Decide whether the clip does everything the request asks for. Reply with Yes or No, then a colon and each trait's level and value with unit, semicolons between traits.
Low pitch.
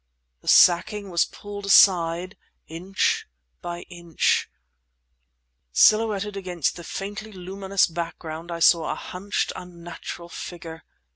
No: medium, 180 Hz